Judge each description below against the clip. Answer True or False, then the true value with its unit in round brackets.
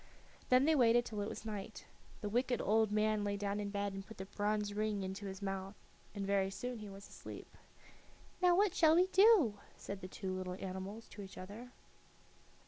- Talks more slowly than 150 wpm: False (200 wpm)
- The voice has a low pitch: False (205 Hz)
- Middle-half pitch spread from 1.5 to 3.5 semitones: True (2.7 semitones)